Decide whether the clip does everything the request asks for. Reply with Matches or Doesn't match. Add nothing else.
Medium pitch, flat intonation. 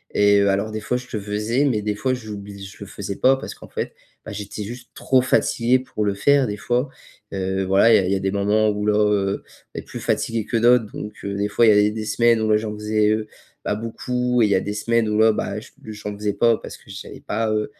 Doesn't match